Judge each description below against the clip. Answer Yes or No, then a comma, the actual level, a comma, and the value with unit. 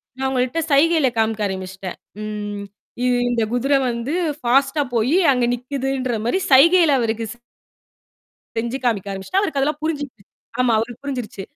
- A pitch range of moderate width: Yes, average, 3.9 semitones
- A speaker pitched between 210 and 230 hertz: No, very high, 250 Hz